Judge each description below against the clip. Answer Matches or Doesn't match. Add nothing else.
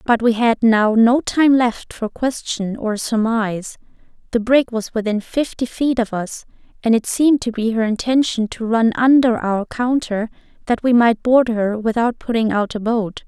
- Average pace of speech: Matches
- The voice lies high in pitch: Matches